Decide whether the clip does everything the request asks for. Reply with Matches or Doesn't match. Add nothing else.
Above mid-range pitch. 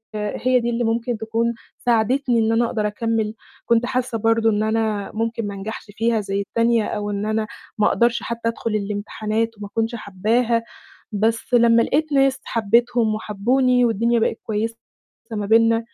Matches